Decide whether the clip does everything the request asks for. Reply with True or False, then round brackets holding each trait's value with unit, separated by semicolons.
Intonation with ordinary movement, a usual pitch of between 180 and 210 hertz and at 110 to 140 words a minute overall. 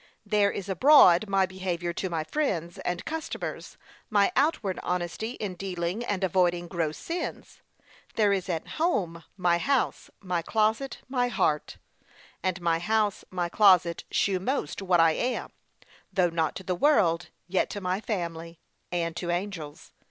False (3.5 semitones; 185 Hz; 150 wpm)